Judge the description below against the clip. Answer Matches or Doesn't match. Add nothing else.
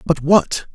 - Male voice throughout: Matches